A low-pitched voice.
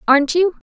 No: very high, 320 Hz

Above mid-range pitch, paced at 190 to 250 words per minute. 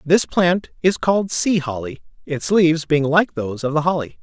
No: medium, 160 Hz; average, 200 wpm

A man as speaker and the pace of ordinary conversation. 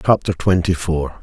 Yes: male; average, 145 wpm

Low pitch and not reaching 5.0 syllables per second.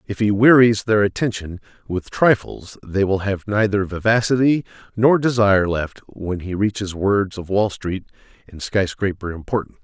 Yes: low, 100 Hz; 4.8 syllables/s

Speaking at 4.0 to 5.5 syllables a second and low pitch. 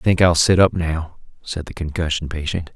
Yes: 5.2 syllables/s; very low, 80 Hz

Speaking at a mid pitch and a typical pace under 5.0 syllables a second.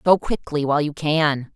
Yes: medium, 150 Hz; 4.8 syllables/s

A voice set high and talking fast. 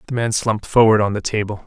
No: low, 110 Hz; fast, 255 wpm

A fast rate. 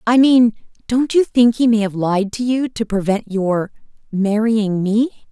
No: average, 170 wpm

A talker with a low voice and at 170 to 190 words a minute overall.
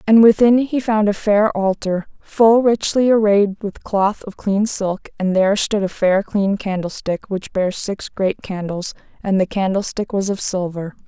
No: high, 200 Hz; average, 180 wpm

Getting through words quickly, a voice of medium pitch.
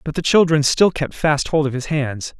Yes: fast, 250 wpm; medium, 150 Hz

